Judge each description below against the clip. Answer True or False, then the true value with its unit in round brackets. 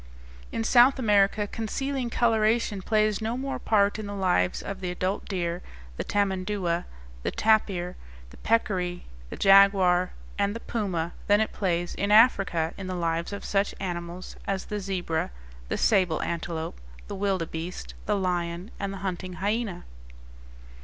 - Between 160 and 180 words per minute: False (150 wpm)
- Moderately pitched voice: False (195 Hz)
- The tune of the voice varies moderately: True (3.0 semitones)